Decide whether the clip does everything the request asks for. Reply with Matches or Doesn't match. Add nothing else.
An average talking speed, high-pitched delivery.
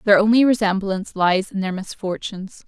Matches